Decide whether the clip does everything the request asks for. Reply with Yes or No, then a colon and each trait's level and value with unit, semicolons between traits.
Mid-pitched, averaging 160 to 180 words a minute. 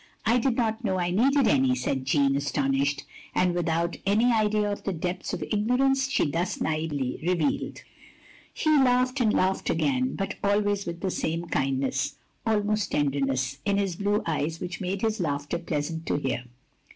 Yes: medium, 175 Hz; average, 175 wpm